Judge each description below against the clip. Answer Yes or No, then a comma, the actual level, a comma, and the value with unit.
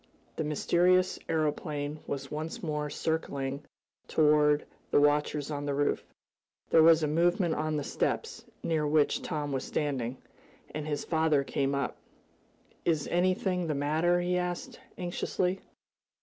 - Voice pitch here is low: No, medium, 155 Hz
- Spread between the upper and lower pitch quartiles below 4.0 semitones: Yes, average, 2.8 semitones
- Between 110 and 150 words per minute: Yes, slow, 135 wpm